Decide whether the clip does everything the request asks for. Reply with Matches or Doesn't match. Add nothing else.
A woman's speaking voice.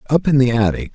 Doesn't match